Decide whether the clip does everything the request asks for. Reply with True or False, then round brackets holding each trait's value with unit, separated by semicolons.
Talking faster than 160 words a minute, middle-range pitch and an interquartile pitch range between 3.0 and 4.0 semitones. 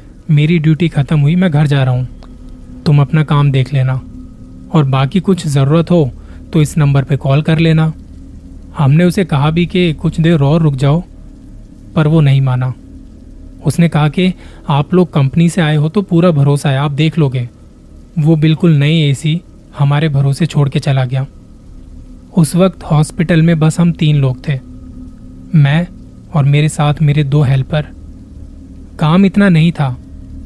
True (170 wpm; 150 Hz; 3.3 semitones)